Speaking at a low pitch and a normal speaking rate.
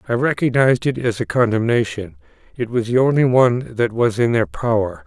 Yes: low, 120 Hz; average, 190 wpm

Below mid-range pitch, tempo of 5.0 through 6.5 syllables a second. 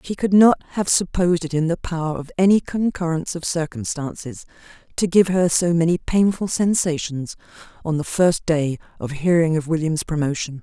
No: medium, 165 Hz; 5.2 syllables/s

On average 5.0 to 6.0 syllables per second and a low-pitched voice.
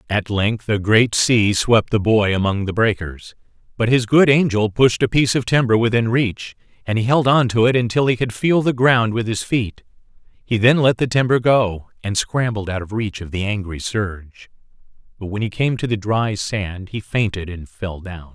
No: 4.8 syllables/s; low, 110 Hz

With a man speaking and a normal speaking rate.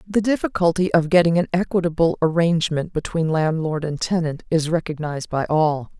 No: female; average, 150 wpm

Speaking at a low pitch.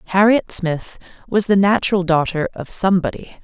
No: high, 190 Hz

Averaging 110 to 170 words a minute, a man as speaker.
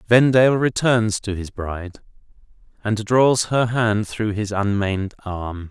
Yes: slow, 135 wpm; male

